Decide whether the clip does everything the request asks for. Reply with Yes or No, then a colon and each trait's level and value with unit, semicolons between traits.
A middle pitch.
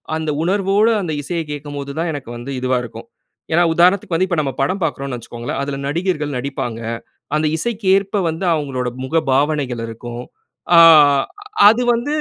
Yes: medium, 150 Hz